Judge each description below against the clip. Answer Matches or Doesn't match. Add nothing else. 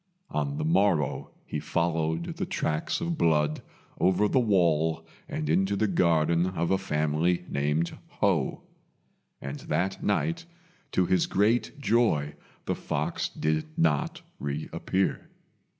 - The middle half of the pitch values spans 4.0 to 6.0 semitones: Matches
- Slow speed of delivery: Matches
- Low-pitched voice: Matches